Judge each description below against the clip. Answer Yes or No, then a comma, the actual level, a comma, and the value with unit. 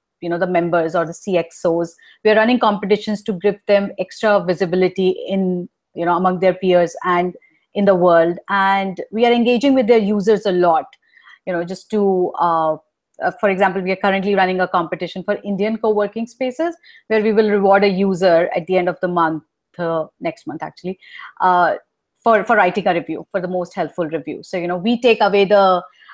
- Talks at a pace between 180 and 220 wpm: Yes, average, 195 wpm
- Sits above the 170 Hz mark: Yes, high, 190 Hz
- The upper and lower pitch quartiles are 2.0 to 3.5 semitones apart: Yes, average, 2.7 semitones